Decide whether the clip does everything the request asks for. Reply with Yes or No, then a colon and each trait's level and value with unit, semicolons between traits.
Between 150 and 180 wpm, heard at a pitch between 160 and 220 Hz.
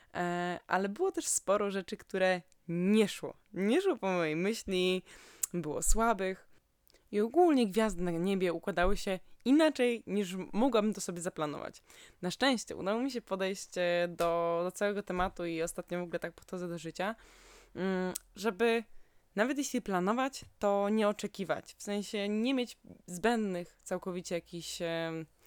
No: average, 140 wpm; high, 190 Hz